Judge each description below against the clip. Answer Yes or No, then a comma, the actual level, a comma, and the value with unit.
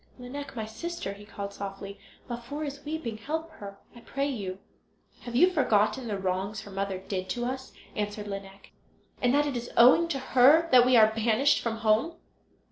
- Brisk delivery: No, average, 185 wpm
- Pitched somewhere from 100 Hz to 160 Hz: No, high, 235 Hz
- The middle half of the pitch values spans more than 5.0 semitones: Yes, wide, 5.4 semitones